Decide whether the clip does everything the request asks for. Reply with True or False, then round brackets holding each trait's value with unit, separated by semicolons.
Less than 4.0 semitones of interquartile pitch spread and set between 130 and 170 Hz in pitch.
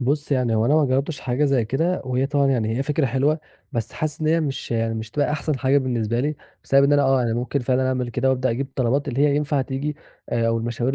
True (3.0 semitones; 135 Hz)